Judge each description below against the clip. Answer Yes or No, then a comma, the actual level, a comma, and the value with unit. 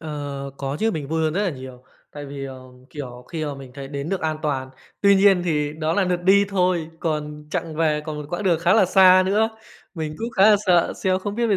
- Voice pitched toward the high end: No, medium, 160 Hz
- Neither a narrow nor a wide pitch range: Yes, average, 4.4 semitones